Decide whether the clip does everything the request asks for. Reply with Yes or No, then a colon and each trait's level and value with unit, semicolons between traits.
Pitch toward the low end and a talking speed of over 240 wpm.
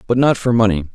Yes: low, 110 Hz; fast, 255 wpm